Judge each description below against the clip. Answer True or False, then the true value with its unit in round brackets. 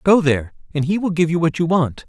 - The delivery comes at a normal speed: False (290 wpm)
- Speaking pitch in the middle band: True (160 Hz)